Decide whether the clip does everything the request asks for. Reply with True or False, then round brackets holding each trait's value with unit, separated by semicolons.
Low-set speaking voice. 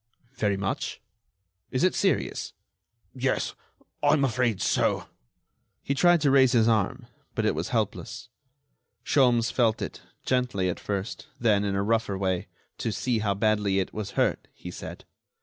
True (115 Hz)